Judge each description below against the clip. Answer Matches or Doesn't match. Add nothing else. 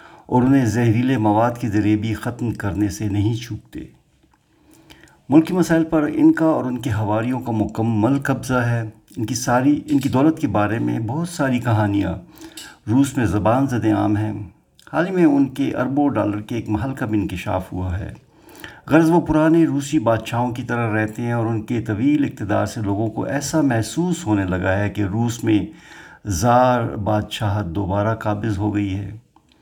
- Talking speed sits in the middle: Matches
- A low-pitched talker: Matches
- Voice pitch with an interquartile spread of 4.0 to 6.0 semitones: Matches